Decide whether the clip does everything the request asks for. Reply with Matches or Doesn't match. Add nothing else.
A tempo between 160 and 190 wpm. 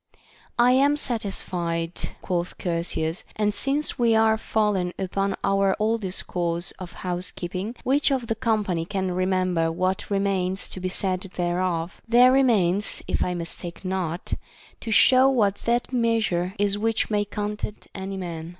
Doesn't match